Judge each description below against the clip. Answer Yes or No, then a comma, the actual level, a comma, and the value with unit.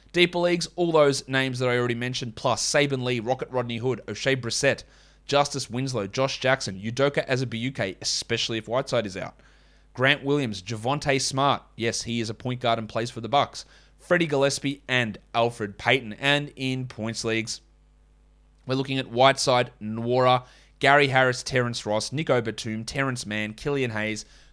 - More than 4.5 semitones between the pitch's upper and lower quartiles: No, average, 3.2 semitones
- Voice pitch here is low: Yes, low, 125 Hz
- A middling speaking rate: Yes, average, 165 wpm